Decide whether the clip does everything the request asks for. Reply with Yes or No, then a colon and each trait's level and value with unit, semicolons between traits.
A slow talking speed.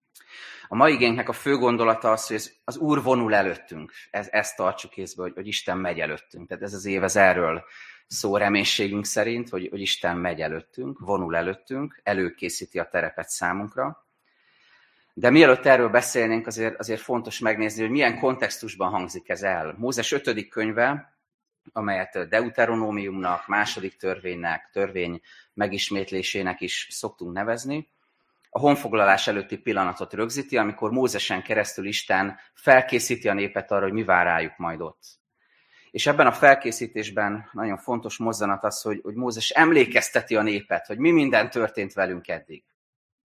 No: average, 145 wpm